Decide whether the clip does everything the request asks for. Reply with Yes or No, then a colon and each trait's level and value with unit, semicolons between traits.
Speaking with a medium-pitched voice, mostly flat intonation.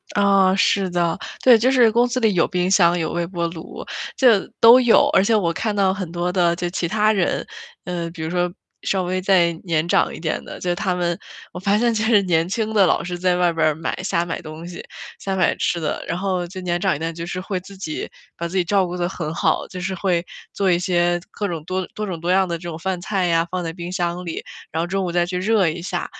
Yes: medium, 180 Hz; narrow, 2.2 semitones